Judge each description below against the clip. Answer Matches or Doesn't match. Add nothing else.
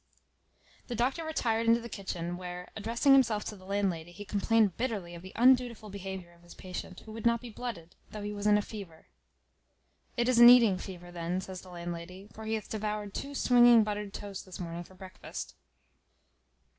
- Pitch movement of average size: Matches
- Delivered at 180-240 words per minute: Matches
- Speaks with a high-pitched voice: Matches